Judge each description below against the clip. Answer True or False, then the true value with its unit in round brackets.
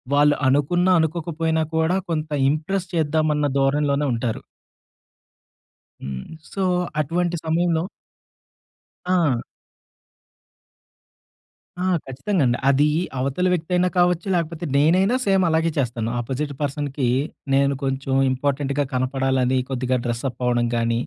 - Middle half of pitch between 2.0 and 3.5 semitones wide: False (3.9 semitones)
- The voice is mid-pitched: True (145 Hz)